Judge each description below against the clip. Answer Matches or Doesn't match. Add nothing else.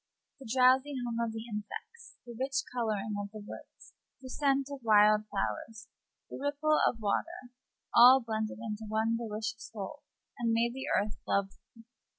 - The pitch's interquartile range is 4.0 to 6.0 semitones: Doesn't match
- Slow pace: Doesn't match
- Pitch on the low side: Doesn't match